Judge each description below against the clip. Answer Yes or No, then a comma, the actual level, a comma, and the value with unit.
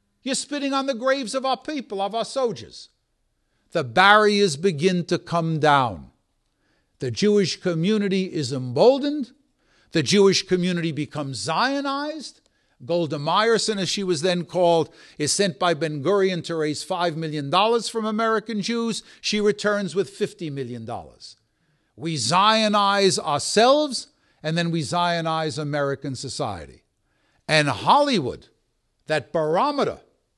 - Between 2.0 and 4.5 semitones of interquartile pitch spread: No, wide, 5.6 semitones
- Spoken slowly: Yes, slow, 125 wpm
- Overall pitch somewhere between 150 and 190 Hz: Yes, medium, 185 Hz